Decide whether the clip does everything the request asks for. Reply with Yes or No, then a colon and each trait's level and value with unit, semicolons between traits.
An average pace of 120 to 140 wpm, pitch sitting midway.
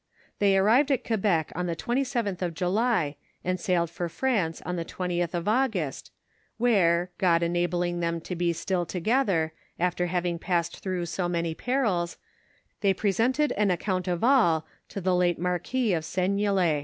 No: average, 165 wpm; medium, 180 Hz